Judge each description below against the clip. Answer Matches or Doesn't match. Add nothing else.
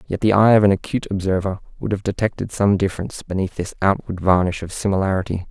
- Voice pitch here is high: Doesn't match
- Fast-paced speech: Doesn't match